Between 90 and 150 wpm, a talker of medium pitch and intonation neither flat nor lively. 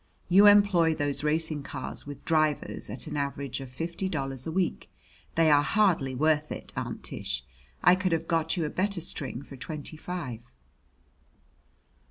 No: average, 165 wpm; medium, 155 Hz; average, 3.6 semitones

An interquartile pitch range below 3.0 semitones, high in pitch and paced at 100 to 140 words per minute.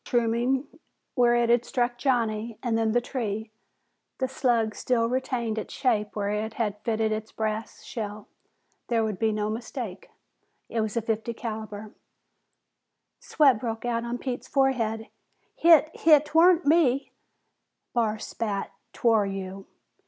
Yes: narrow, 2.4 semitones; high, 230 Hz; slow, 135 wpm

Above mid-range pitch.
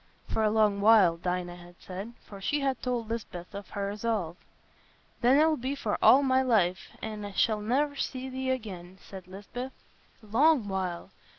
Yes: high, 215 Hz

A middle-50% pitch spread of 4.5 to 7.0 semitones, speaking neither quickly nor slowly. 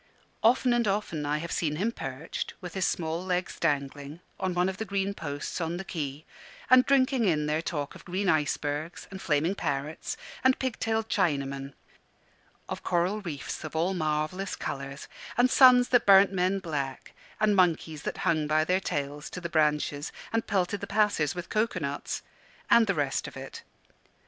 Yes: average, 4.9 semitones; average, 180 wpm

